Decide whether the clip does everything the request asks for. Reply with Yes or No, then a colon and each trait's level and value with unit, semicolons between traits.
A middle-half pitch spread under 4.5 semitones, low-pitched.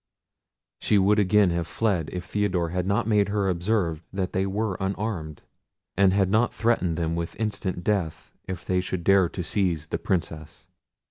Yes: average, 3.1 semitones; very low, 95 Hz